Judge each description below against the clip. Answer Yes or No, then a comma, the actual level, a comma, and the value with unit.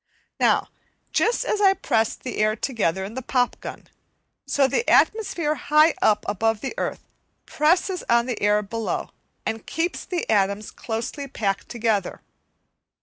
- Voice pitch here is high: Yes, high, 235 Hz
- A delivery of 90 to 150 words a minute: Yes, average, 145 wpm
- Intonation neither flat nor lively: No, wide, 6.2 semitones